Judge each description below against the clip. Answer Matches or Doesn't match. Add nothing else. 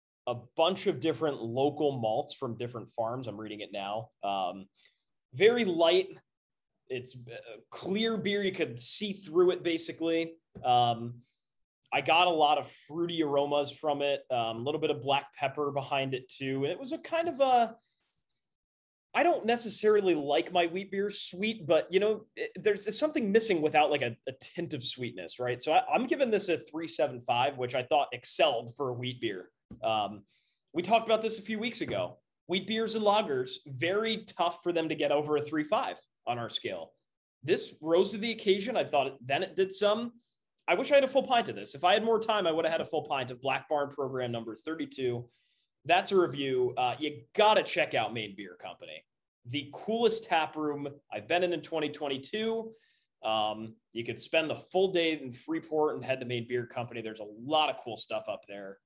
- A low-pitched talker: Doesn't match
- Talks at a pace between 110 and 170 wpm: Doesn't match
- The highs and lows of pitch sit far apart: Matches